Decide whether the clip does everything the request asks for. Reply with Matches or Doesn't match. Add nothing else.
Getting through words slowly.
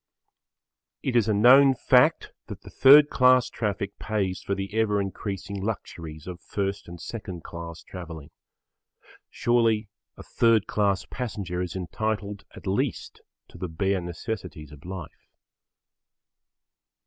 Matches